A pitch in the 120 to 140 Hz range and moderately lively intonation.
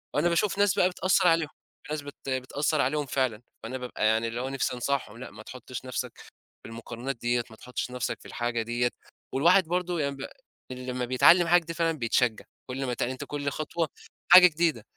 Yes: low, 130 Hz; average, 4.9 semitones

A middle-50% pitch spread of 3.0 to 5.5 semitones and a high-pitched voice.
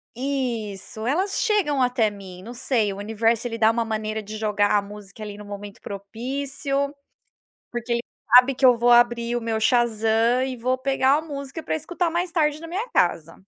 Yes: average, 4.1 semitones; high, 240 Hz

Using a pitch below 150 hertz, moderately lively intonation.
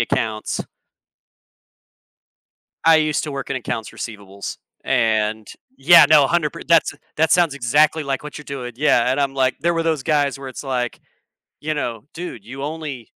Yes: medium, 140 Hz; average, 4.1 semitones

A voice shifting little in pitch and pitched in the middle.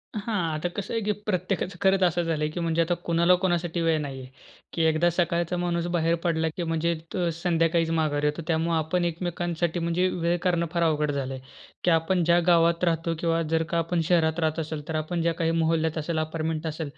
Yes: narrow, 1.5 semitones; medium, 165 Hz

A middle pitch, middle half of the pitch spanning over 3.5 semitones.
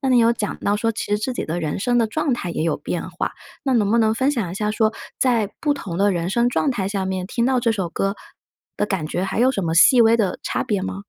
No: high, 210 Hz; average, 4.0 semitones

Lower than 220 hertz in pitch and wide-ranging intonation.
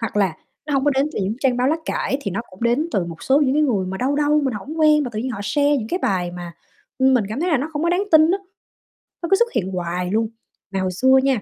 No: very high, 255 Hz; wide, 7.1 semitones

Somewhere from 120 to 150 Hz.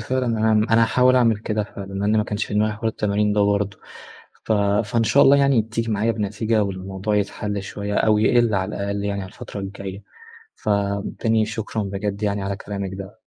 No: low, 105 Hz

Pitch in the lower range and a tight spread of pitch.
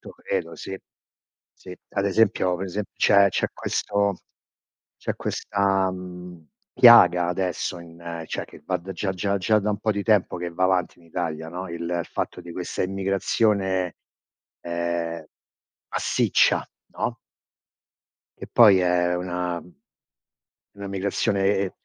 Yes: very low, 90 Hz; narrow, 2.2 semitones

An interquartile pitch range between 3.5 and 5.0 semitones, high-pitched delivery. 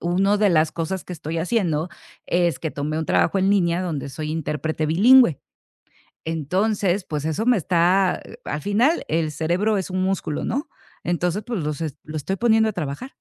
No: average, 4.2 semitones; medium, 175 Hz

